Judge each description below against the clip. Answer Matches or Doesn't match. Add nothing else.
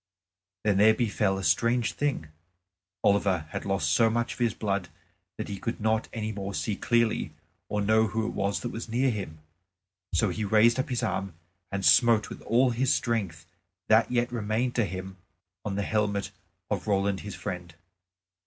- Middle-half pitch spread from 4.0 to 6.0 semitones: Doesn't match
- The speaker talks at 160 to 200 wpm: Matches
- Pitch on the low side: Matches